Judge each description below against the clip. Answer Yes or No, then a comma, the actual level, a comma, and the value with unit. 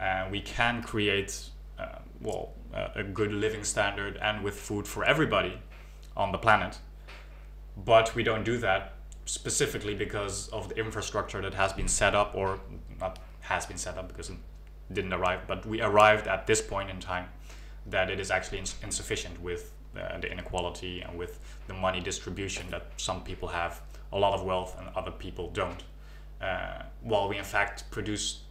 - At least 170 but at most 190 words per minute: Yes, average, 180 wpm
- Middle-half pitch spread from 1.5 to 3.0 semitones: Yes, narrow, 2.4 semitones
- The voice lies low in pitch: Yes, very low, 95 Hz